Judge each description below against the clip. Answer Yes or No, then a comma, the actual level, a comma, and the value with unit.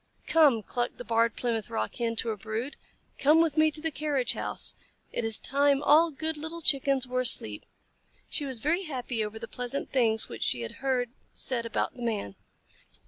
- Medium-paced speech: Yes, average, 195 wpm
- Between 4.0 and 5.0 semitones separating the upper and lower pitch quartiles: Yes, average, 4.4 semitones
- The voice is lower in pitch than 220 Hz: No, very high, 255 Hz